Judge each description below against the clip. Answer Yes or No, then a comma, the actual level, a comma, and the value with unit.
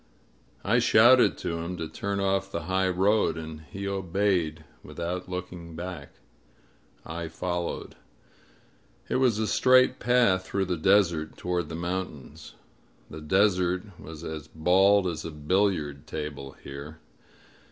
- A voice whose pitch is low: Yes, very low, 90 Hz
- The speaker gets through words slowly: Yes, slow, 130 wpm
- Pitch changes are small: No, average, 3.5 semitones